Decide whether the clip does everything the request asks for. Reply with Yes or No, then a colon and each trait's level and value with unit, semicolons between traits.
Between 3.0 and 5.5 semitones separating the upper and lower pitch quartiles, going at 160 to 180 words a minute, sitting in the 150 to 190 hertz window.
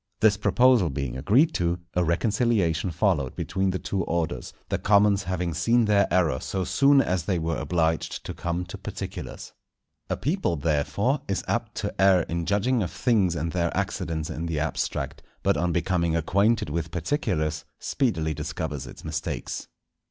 No: average, 4.0 semitones; average, 165 wpm; very low, 90 Hz